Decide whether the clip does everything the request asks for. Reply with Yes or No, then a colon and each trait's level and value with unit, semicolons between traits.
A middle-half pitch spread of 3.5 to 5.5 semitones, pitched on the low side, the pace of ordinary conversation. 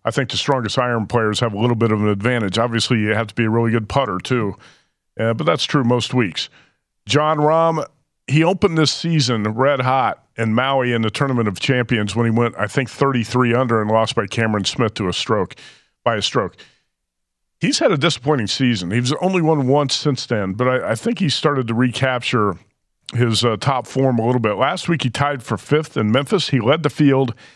No: average, 3.8 semitones; low, 125 Hz; fast, 220 wpm